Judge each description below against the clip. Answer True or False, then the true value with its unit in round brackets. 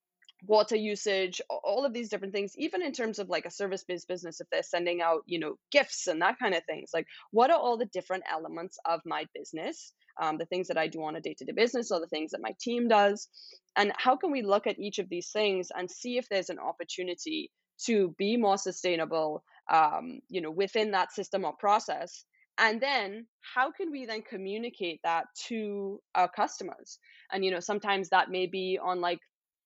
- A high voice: True (200 Hz)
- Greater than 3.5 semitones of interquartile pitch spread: True (4.4 semitones)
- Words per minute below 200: False (205 wpm)